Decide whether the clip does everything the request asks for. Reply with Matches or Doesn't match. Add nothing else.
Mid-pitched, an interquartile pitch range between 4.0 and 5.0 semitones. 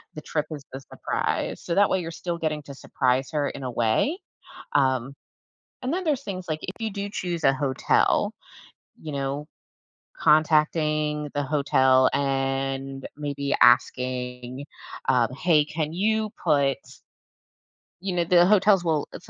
Matches